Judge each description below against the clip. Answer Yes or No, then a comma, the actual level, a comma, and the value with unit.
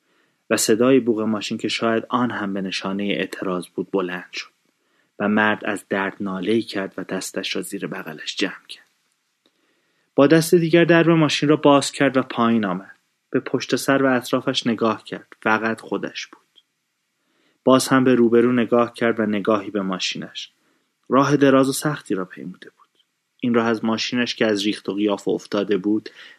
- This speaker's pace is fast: Yes, fast, 175 wpm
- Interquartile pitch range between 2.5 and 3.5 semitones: No, average, 4.2 semitones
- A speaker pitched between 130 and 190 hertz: No, low, 115 Hz